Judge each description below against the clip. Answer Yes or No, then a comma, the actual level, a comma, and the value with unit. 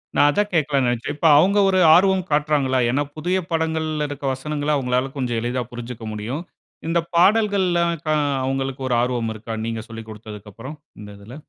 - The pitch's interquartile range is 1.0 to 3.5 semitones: No, average, 5.1 semitones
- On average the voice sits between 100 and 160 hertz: Yes, low, 135 Hz